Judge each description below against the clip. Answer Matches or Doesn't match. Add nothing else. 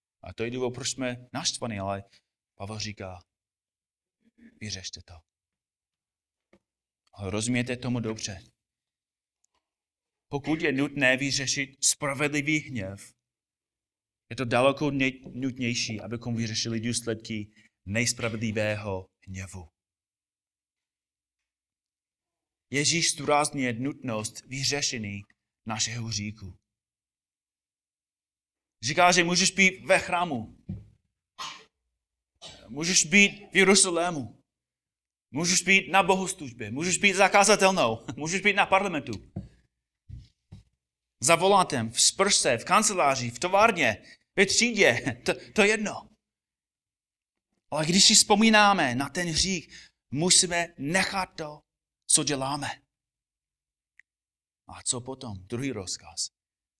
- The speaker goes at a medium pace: Doesn't match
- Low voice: Matches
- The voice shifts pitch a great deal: Matches